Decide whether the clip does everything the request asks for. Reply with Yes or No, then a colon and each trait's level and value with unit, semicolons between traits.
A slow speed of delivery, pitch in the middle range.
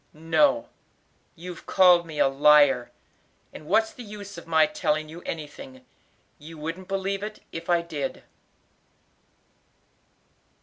Yes: slow, 125 wpm; medium, 165 Hz